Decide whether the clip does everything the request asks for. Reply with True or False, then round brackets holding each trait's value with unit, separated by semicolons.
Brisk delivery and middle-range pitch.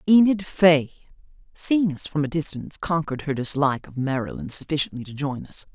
False (165 wpm; 150 Hz)